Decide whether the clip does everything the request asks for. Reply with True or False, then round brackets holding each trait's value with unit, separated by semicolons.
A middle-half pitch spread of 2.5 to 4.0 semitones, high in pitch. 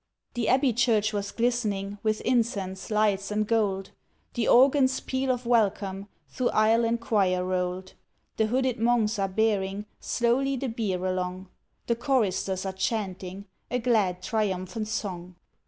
True (3.6 semitones; 215 Hz)